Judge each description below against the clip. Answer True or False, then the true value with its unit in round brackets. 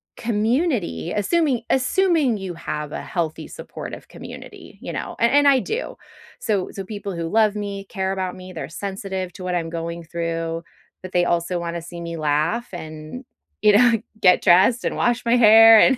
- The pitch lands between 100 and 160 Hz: False (190 Hz)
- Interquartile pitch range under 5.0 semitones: False (5.4 semitones)